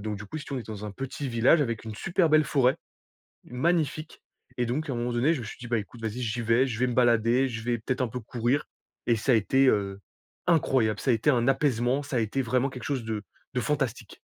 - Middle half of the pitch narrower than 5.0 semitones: Yes, average, 3.2 semitones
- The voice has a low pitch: Yes, low, 125 Hz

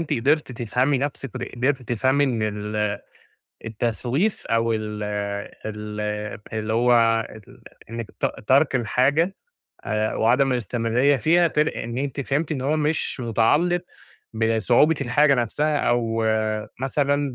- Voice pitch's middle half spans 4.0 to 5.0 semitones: Yes, average, 4.3 semitones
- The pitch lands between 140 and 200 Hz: No, low, 125 Hz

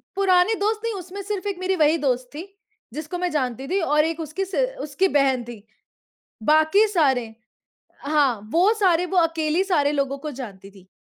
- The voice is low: No, very high, 315 Hz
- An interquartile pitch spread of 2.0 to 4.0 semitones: No, wide, 5.6 semitones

